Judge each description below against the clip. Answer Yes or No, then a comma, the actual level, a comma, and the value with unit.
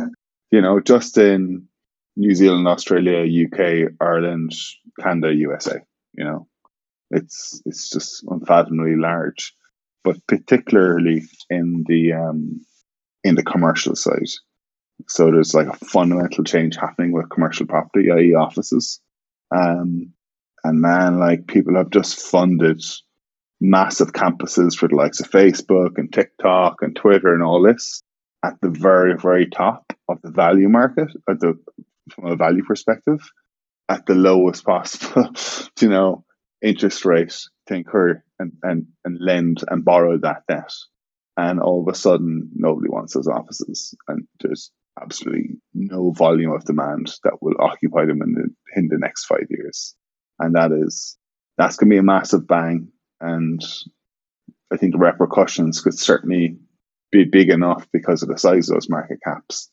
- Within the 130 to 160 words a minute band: Yes, average, 150 wpm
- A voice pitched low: Yes, very low, 85 Hz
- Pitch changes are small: Yes, narrow, 2.3 semitones